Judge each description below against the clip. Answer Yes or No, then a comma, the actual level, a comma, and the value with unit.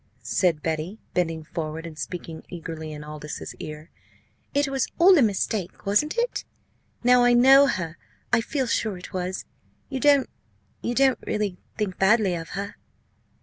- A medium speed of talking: Yes, average, 155 wpm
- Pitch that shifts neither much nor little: No, wide, 7.2 semitones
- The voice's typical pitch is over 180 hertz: Yes, high, 190 Hz